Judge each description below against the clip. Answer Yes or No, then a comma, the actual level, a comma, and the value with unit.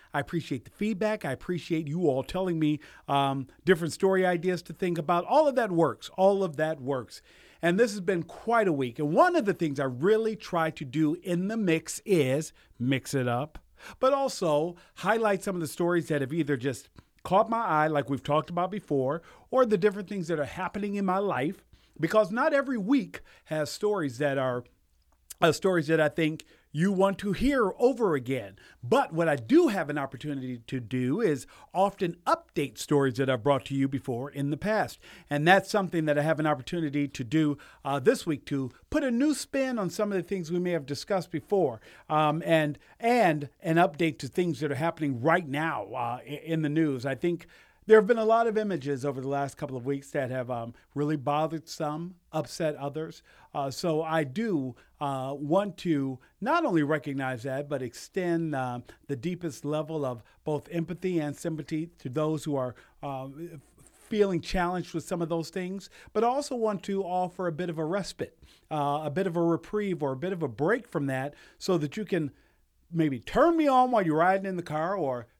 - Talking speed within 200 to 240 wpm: Yes, fast, 205 wpm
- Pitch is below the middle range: No, medium, 160 Hz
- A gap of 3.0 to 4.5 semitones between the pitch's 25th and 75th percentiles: No, average, 5.0 semitones